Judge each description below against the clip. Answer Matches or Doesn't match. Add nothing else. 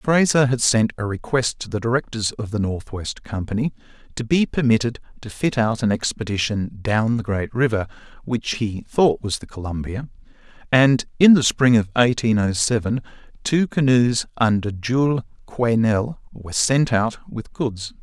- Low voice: Matches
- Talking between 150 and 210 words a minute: Matches